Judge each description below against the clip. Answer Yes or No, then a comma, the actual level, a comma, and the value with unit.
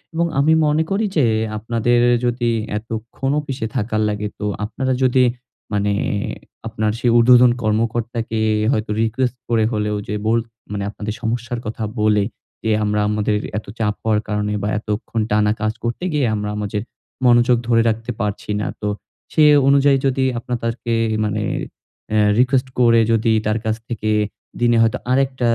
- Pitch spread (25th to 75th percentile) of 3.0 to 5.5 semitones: No, narrow, 2.6 semitones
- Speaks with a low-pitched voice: Yes, low, 115 Hz